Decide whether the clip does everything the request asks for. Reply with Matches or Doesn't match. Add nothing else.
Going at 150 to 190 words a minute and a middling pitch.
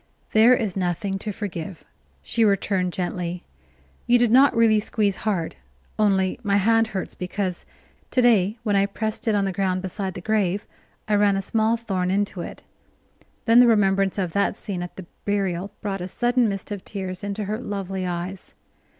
Doesn't match